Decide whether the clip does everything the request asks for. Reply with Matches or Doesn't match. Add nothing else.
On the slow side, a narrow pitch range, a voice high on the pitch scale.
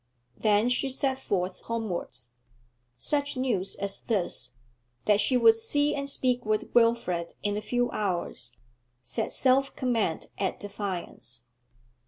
Doesn't match